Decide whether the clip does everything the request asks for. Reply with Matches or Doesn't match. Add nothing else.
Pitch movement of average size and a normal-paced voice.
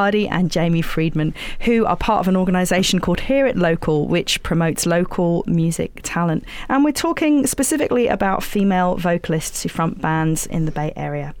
Matches